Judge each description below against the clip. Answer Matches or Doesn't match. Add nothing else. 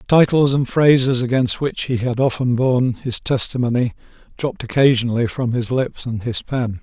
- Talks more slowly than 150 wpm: Doesn't match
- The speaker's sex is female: Doesn't match